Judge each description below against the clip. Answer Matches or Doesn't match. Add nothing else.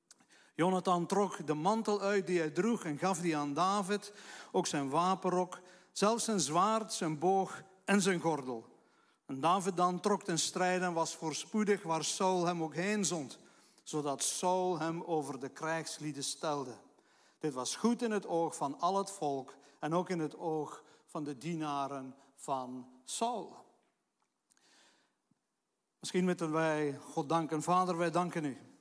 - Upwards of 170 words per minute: Doesn't match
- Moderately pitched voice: Matches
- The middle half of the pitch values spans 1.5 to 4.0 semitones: Matches